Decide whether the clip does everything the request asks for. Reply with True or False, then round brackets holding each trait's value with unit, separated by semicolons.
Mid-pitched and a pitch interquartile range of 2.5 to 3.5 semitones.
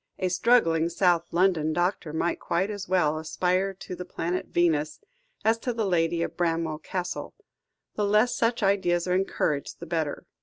True (175 Hz; 2.9 semitones)